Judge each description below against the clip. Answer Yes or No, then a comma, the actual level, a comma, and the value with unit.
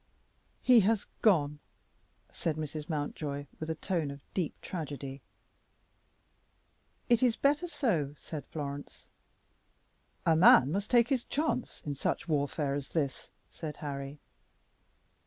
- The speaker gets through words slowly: Yes, slow, 120 wpm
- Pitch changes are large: Yes, wide, 6.1 semitones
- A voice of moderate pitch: Yes, medium, 155 Hz